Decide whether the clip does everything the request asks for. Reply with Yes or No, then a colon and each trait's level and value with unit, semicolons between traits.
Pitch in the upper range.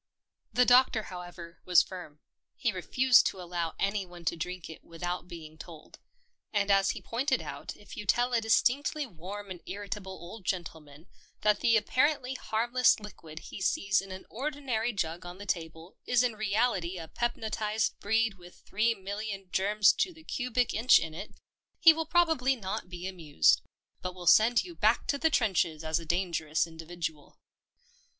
Yes: high, 195 Hz